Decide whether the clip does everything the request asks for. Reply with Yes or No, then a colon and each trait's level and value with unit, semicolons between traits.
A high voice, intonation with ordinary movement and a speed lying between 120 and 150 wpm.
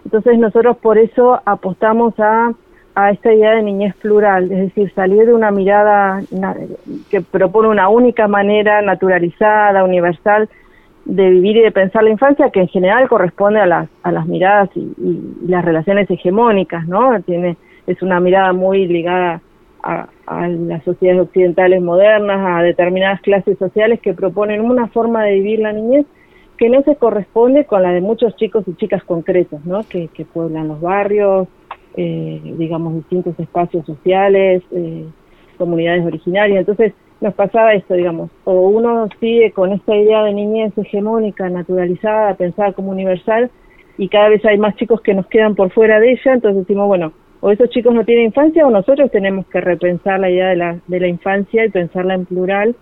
No: high, 195 Hz; average, 3.2 semitones; average, 175 wpm